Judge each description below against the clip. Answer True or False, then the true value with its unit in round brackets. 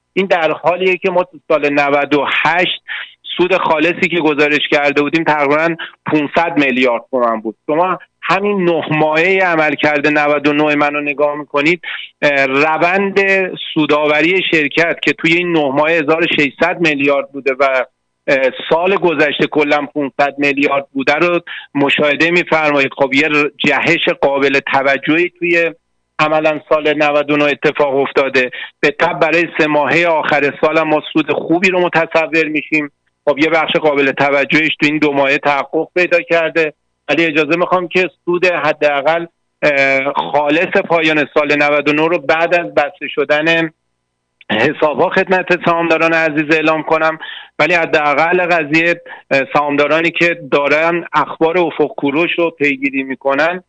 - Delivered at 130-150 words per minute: True (135 wpm)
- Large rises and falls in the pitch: False (2.5 semitones)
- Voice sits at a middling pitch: True (155 Hz)